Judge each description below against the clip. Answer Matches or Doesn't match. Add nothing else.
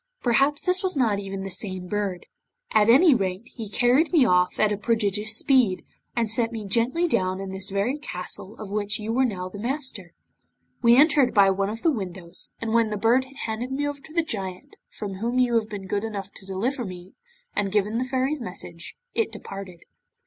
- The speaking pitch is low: Doesn't match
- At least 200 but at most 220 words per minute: Matches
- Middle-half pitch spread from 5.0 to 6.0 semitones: Doesn't match